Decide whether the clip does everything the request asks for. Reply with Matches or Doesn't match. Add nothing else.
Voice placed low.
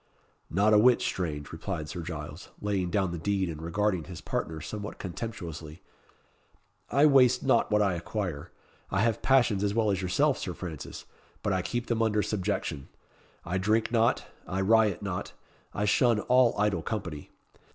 Matches